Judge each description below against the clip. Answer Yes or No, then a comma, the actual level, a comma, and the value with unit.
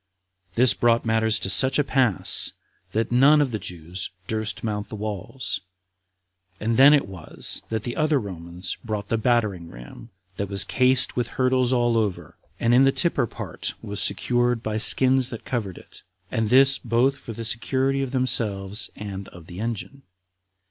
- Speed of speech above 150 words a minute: Yes, average, 170 wpm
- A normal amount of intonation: Yes, average, 3.9 semitones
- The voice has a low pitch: Yes, low, 115 Hz